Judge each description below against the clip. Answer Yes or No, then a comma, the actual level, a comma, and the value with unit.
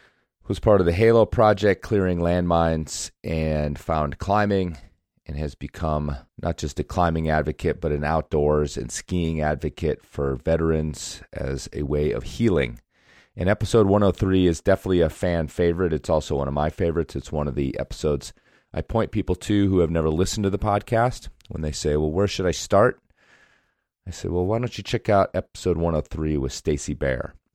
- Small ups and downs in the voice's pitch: No, average, 4.5 semitones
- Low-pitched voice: Yes, very low, 80 Hz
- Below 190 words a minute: Yes, average, 180 wpm